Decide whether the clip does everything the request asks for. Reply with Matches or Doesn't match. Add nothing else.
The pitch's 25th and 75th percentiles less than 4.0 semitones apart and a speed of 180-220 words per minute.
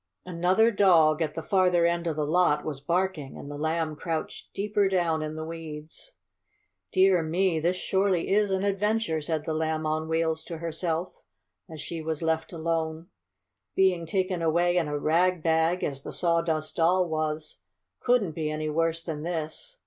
Doesn't match